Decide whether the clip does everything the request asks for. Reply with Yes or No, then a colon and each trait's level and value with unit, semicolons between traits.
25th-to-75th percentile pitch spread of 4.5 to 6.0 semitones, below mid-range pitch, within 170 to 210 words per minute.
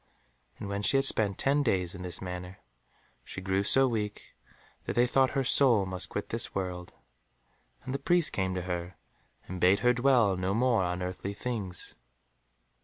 Yes: average, 5.2 semitones; low, 100 Hz; average, 180 wpm